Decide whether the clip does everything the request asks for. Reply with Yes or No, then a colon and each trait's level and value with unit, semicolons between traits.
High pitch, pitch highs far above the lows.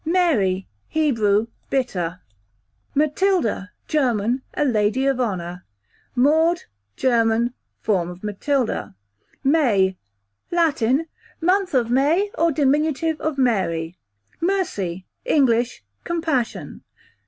Yes: very high, 250 Hz; wide, 7.1 semitones